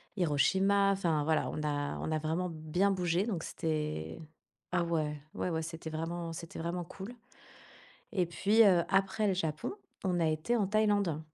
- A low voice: No, medium, 170 Hz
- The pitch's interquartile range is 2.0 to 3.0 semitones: No, average, 3.6 semitones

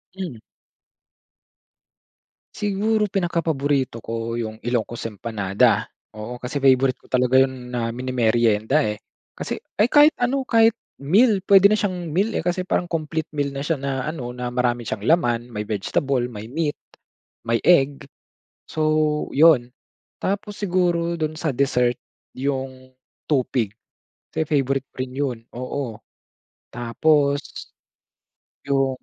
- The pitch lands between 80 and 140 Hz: Yes, low, 135 Hz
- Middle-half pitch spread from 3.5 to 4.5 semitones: No, wide, 5.5 semitones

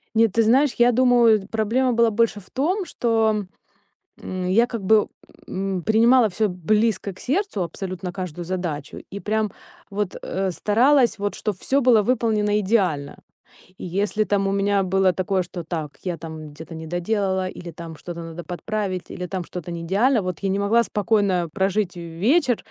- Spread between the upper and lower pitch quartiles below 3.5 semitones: No, average, 3.8 semitones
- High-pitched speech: Yes, high, 200 Hz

